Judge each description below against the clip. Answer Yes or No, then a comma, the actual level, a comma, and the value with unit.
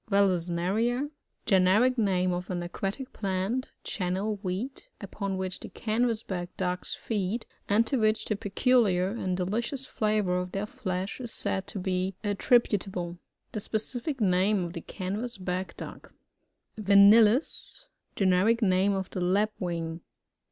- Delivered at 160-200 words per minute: No, average, 140 wpm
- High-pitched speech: Yes, high, 195 Hz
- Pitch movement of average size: Yes, average, 3.3 semitones